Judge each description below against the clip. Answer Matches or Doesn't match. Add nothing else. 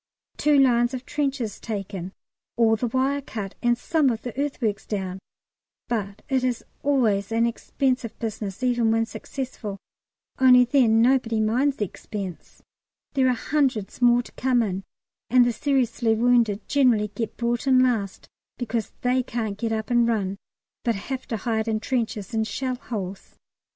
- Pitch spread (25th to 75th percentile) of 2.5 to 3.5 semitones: Matches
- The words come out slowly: Doesn't match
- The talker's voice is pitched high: Matches